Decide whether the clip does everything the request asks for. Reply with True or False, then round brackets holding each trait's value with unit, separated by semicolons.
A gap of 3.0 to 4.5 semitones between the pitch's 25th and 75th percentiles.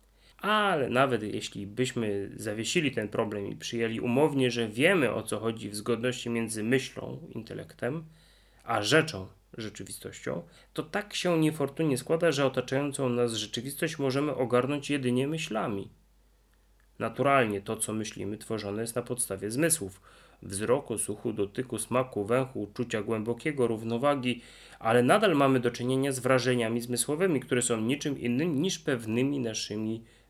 True (3.3 semitones)